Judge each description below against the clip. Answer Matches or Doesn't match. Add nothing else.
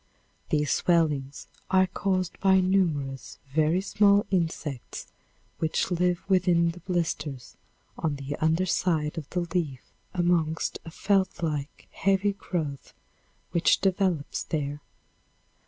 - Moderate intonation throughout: Matches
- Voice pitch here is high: Doesn't match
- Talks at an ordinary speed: Doesn't match